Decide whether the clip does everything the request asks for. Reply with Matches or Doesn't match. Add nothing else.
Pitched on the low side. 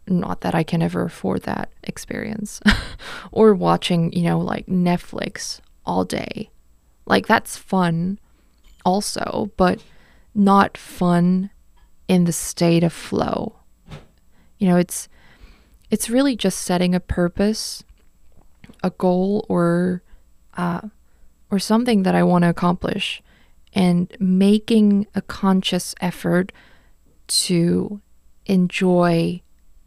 Doesn't match